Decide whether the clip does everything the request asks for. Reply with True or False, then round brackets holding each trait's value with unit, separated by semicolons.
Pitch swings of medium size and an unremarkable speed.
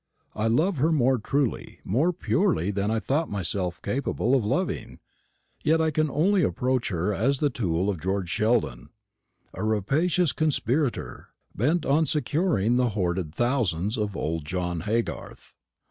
False (7.2 semitones; 145 wpm)